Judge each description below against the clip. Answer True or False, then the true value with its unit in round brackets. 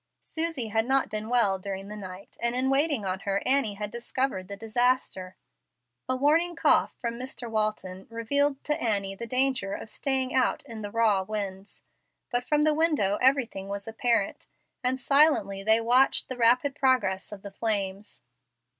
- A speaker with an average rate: True (170 wpm)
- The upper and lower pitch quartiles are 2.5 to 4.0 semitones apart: False (4.7 semitones)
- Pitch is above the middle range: True (230 Hz)